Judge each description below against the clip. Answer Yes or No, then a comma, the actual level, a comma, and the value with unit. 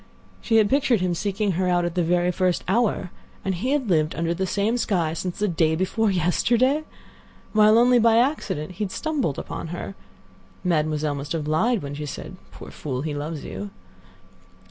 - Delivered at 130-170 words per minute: No, average, 180 wpm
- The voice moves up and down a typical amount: No, wide, 5.7 semitones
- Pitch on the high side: No, medium, 180 Hz